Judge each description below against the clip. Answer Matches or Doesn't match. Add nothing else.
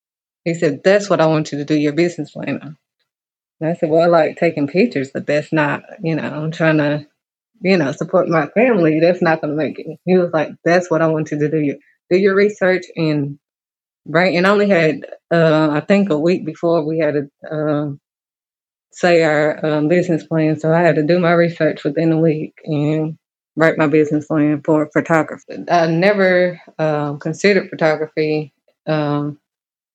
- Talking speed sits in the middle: Matches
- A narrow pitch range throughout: Matches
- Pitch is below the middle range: Doesn't match